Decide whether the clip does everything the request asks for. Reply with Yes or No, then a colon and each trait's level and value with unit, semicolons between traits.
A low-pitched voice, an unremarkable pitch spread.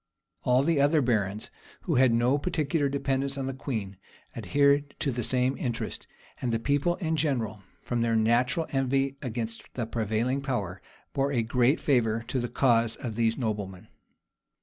Yes: low, 125 Hz; average, 3.5 semitones